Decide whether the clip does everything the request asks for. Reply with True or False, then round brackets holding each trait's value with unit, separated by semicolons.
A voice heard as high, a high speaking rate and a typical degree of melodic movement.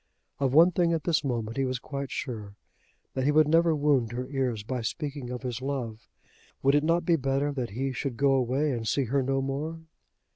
False (135 Hz; 215 wpm; 3.0 semitones)